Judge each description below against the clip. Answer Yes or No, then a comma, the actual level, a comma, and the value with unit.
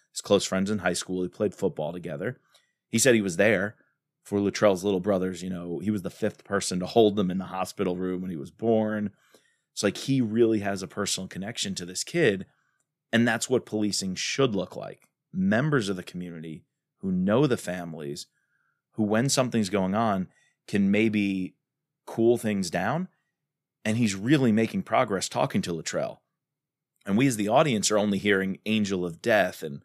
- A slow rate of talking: No, average, 185 wpm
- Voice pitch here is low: Yes, low, 105 Hz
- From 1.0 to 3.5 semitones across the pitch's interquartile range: No, average, 4.3 semitones